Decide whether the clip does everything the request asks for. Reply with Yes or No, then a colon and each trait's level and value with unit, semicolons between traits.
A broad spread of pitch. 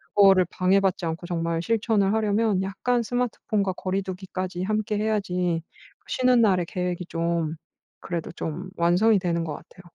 No: average, 3.3 semitones